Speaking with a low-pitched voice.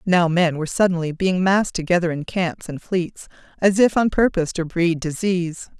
No: medium, 175 Hz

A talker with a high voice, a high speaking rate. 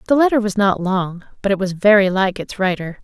Yes: high, 200 Hz; fast, 235 wpm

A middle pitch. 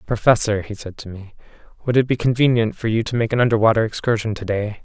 No: low, 110 Hz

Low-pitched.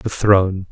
Yes: low, 100 Hz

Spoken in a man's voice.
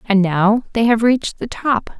No: female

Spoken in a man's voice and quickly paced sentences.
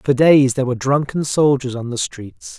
Yes: male; fast, 210 wpm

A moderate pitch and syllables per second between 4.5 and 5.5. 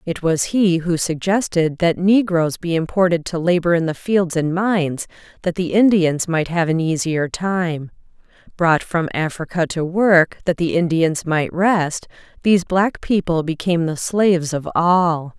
No: medium, 170 Hz; 4.3 syllables/s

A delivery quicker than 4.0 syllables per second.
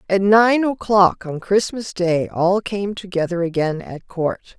No: 3.9 syllables/s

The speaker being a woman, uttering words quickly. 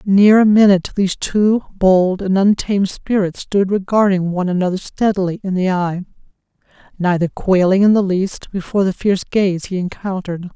No: female; average, 160 wpm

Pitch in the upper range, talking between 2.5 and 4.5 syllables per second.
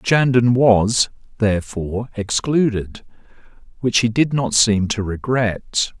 No: low, 115 Hz; 3.8 syllables/s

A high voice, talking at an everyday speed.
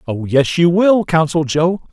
No: medium, 165 Hz; average, 190 wpm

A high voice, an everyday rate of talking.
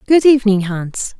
Yes: high, 225 Hz; average, 150 wpm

